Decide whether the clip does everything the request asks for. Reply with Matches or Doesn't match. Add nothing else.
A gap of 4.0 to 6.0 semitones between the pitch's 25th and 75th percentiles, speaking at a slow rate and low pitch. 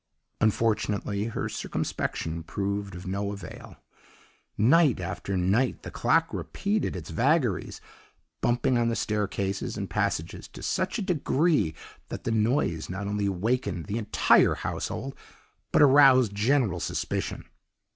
Matches